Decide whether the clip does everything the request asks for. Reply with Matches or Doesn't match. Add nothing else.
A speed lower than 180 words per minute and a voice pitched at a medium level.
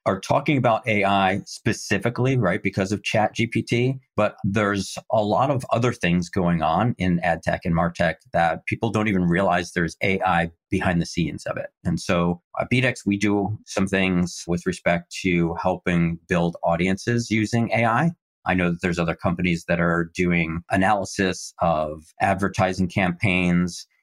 Doesn't match